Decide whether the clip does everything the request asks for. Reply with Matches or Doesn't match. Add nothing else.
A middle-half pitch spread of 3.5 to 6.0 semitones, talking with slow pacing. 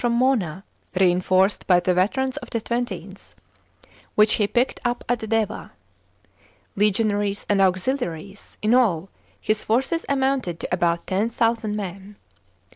Matches